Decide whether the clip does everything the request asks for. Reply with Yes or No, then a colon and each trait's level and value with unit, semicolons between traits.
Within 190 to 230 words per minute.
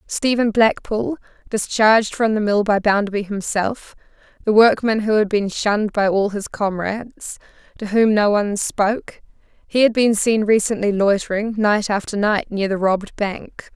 No: average, 155 wpm